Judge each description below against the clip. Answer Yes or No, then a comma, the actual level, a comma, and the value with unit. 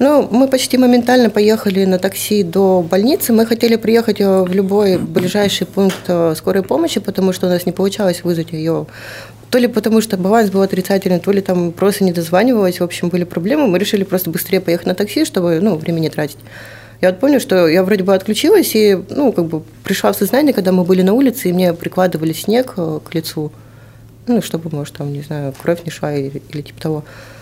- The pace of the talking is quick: Yes, fast, 205 wpm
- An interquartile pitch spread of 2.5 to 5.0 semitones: Yes, average, 4.1 semitones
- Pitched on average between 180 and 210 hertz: Yes, high, 190 Hz